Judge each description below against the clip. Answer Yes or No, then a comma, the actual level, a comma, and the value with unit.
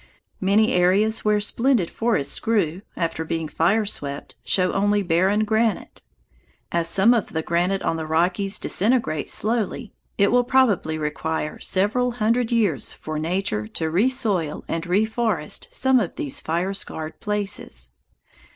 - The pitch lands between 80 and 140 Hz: No, high, 195 Hz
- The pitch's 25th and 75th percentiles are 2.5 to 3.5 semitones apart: No, average, 5.1 semitones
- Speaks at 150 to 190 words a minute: No, average, 140 wpm